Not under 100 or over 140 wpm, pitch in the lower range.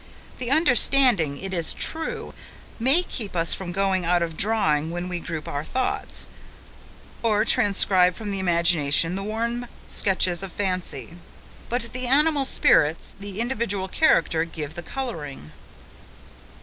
No: slow, 135 wpm; high, 190 Hz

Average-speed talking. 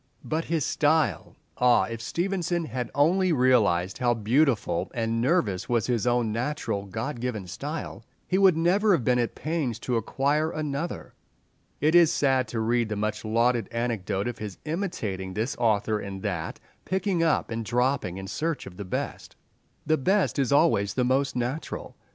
Yes: average, 170 wpm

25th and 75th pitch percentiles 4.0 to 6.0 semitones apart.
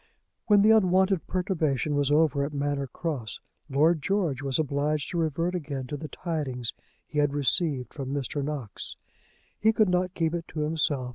No: average, 3.6 semitones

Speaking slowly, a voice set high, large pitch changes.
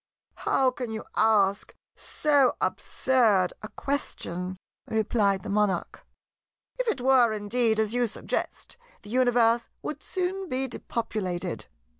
No: slow, 120 wpm; high, 225 Hz; average, 3.9 semitones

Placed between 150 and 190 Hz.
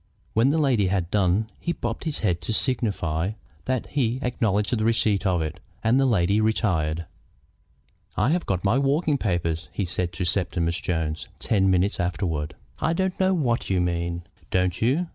No: low, 100 Hz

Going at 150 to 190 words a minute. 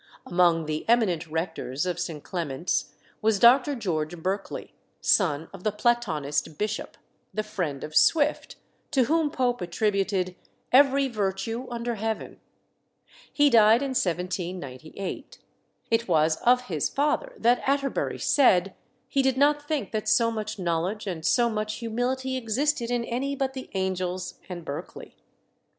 No: average, 140 wpm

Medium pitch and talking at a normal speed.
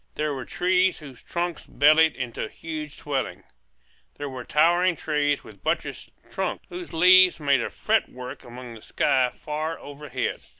Yes: medium, 150 Hz; average, 145 wpm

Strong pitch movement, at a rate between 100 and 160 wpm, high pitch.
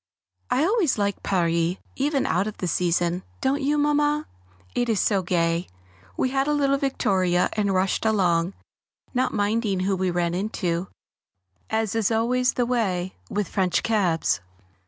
Yes: wide, 5.9 semitones; average, 155 wpm; high, 205 Hz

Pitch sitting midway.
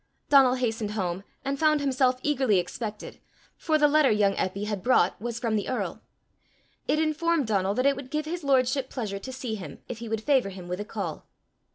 No: very high, 250 Hz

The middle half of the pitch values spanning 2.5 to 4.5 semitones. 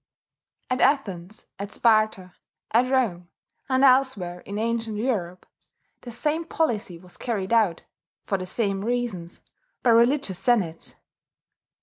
No: average, 4.9 semitones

